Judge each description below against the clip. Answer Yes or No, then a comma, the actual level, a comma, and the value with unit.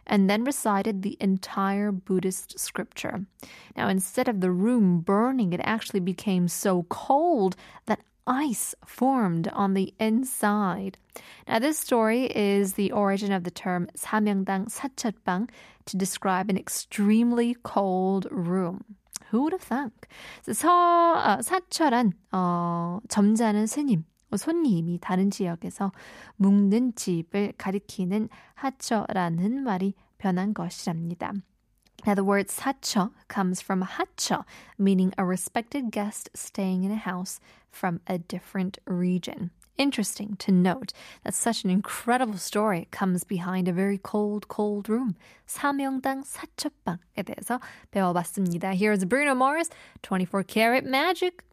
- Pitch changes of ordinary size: Yes, average, 4.0 semitones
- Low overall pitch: No, high, 205 Hz